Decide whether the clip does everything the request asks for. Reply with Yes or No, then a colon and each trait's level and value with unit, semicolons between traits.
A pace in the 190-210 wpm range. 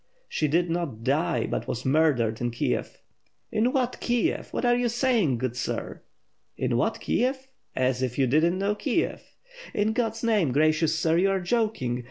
No: average, 180 wpm